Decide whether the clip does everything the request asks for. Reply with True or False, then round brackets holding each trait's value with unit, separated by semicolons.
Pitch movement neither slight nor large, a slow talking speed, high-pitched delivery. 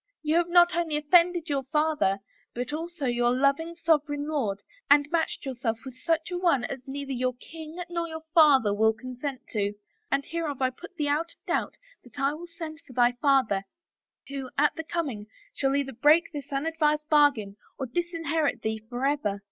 False (4.2 semitones; 190 wpm; 290 Hz)